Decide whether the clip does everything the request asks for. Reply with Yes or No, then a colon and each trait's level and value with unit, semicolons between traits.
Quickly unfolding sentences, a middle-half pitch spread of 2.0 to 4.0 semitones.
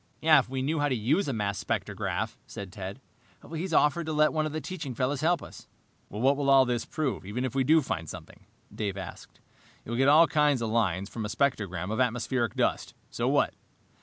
No: fast, 210 wpm; wide, 5.5 semitones